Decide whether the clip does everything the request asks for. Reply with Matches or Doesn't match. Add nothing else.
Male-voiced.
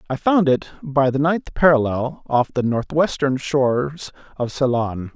Matches